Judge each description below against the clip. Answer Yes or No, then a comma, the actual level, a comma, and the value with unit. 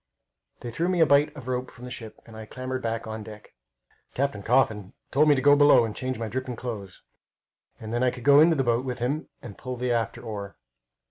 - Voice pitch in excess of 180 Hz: No, low, 125 Hz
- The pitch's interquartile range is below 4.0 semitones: Yes, average, 3.0 semitones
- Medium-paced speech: No, fast, 230 wpm